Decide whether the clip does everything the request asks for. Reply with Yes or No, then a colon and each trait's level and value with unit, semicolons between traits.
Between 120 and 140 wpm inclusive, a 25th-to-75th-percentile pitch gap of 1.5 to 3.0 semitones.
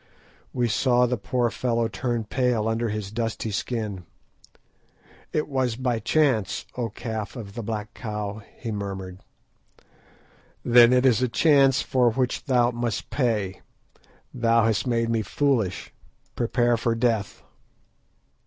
Yes: slow, 135 wpm; narrow, 2.6 semitones